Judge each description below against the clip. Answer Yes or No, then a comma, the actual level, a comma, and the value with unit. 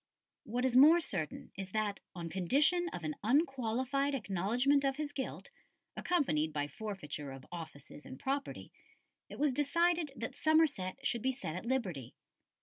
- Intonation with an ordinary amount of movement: No, wide, 8.1 semitones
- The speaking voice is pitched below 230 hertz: No, very high, 250 Hz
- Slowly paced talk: No, average, 155 wpm